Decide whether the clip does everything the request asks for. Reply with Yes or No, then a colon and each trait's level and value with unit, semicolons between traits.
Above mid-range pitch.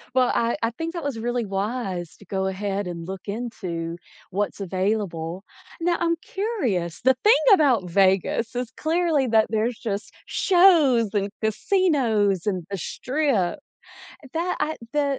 Yes: high, 225 Hz